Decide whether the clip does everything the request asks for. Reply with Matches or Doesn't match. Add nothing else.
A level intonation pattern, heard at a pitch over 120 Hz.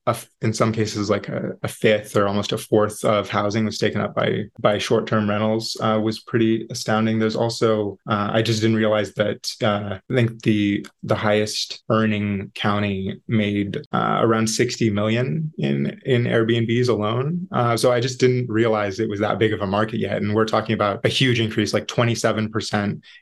Doesn't match